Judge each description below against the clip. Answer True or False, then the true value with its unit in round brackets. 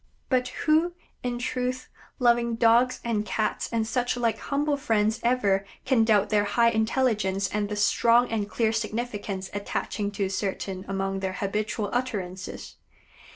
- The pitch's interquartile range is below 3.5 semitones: True (3.1 semitones)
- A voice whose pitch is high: True (220 Hz)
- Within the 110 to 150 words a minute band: True (145 wpm)